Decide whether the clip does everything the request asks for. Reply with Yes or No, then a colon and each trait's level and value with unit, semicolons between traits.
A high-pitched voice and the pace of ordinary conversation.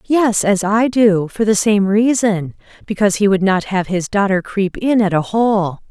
Yes: high, 200 Hz; average, 185 wpm